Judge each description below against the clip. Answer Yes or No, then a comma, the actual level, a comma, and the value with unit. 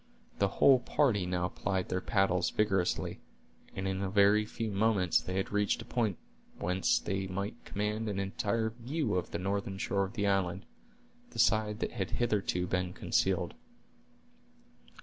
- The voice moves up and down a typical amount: No, narrow, 2.2 semitones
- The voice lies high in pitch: No, low, 100 Hz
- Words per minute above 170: No, average, 160 wpm